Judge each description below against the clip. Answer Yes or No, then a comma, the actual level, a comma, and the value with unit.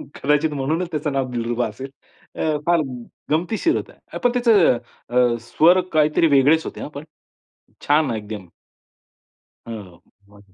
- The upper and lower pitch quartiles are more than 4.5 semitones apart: Yes, average, 5.1 semitones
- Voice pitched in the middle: Yes, medium, 145 Hz